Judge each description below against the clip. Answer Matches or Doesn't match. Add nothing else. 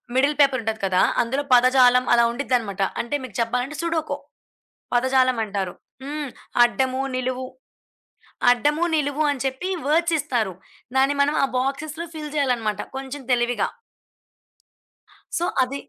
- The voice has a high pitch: Matches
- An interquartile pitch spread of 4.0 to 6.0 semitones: Doesn't match